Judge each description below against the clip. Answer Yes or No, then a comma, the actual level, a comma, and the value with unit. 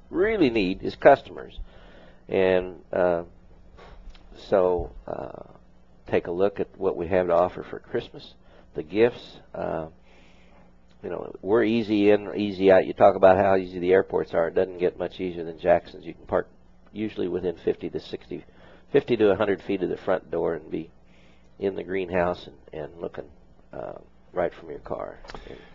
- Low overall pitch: Yes, very low, 90 Hz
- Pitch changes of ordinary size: No, wide, 7.7 semitones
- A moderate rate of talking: Yes, average, 175 wpm